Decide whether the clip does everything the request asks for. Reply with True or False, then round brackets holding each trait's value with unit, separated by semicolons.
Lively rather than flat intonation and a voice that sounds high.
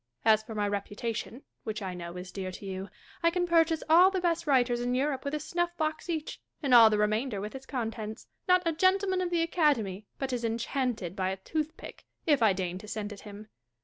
True (7.4 semitones; 240 Hz)